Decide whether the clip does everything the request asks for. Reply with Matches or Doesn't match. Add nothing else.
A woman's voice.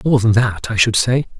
Doesn't match